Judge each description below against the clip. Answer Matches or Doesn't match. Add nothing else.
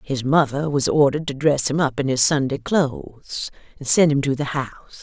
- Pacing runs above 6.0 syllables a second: Doesn't match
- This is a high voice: Doesn't match